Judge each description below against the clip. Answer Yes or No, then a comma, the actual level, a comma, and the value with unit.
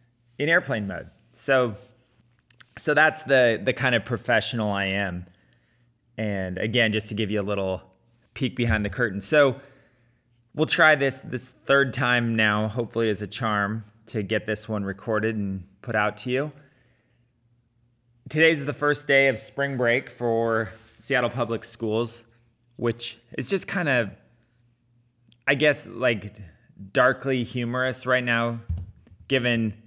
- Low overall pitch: Yes, low, 120 Hz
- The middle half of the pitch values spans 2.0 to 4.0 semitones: Yes, average, 2.7 semitones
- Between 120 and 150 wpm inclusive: Yes, average, 145 wpm